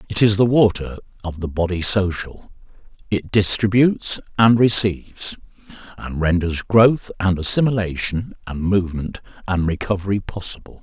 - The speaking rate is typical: No, slow, 120 wpm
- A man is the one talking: Yes, male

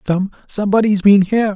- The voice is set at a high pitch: Yes, high, 200 Hz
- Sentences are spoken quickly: No, slow, 115 wpm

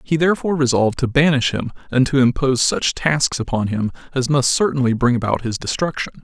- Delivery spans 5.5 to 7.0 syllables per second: Yes, 6.0 syllables/s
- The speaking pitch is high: No, low, 135 Hz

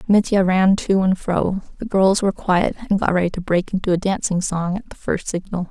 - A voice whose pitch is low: No, high, 190 Hz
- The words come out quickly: Yes, fast, 230 wpm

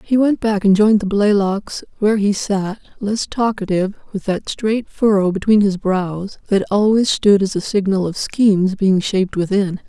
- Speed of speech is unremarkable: Yes, average, 180 wpm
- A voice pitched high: Yes, high, 200 Hz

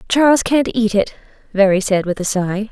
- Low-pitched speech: No, high, 215 Hz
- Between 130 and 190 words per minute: No, average, 200 wpm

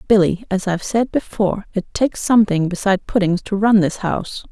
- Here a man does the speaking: No, female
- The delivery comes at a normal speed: Yes, average, 185 wpm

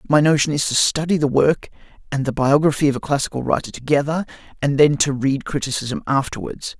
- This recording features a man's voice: Yes, male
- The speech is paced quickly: No, average, 185 wpm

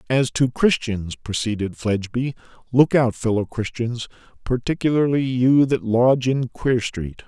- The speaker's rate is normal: No, slow, 130 wpm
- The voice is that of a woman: No, male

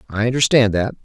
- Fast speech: No, average, 175 wpm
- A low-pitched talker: Yes, low, 115 Hz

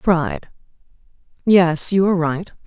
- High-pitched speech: No, medium, 170 Hz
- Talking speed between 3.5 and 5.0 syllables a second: Yes, 4.4 syllables/s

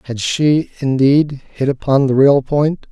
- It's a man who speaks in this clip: Yes, male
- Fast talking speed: No, average, 165 wpm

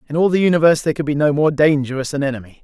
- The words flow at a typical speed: No, fast, 275 wpm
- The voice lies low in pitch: No, medium, 150 Hz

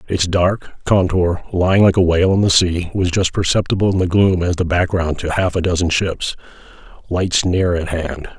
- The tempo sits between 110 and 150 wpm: No, average, 200 wpm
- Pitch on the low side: Yes, very low, 90 Hz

